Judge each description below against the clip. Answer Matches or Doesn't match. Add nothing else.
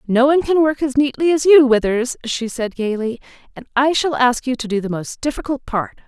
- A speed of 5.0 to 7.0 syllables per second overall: Matches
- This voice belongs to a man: Doesn't match